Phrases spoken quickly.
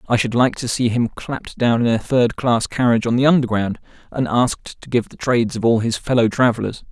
Yes: fast, 235 wpm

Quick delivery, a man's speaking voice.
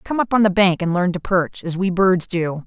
No: fast, 295 wpm; female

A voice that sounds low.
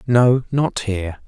Yes: low, 115 Hz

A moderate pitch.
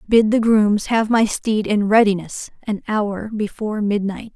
No: high, 210 Hz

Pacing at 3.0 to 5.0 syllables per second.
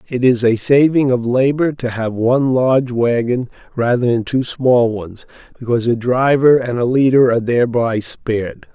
Yes: 4.9 syllables/s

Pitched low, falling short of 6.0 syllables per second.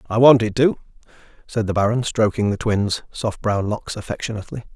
Yes: low, 110 Hz; 5.7 syllables/s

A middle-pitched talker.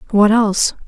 No: high, 210 Hz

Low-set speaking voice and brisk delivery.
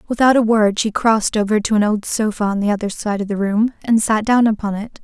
No: high, 215 Hz; fast, 260 wpm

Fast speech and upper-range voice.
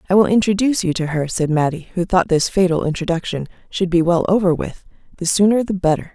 No: fast, 215 wpm; medium, 180 Hz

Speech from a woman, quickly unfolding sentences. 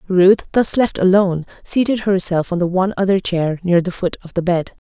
Yes: female; fast, 210 wpm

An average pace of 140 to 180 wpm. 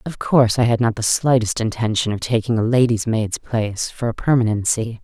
No: fast, 205 wpm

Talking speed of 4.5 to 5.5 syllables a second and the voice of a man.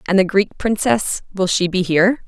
No: 5.3 syllables/s; female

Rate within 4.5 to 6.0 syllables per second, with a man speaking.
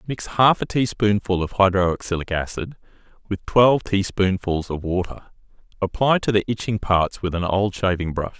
Yes: 5.0 syllables/s; male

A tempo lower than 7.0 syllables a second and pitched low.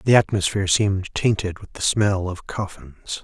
Yes: 4.9 syllables/s; very low, 95 Hz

